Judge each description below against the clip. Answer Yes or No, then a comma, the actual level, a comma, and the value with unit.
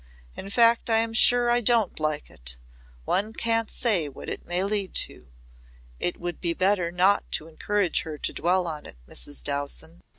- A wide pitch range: Yes, wide, 5.7 semitones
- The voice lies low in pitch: No, medium, 185 Hz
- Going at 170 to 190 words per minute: Yes, average, 175 wpm